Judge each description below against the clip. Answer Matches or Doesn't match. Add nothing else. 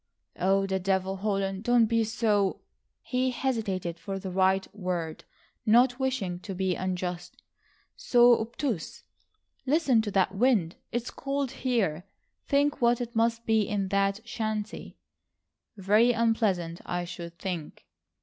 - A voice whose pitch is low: Doesn't match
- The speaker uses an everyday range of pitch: Matches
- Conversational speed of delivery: Doesn't match